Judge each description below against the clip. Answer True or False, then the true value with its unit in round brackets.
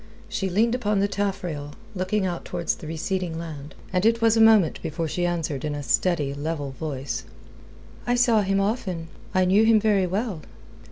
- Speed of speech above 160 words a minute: True (180 wpm)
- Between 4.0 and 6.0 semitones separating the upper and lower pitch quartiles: True (5.0 semitones)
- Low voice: False (180 Hz)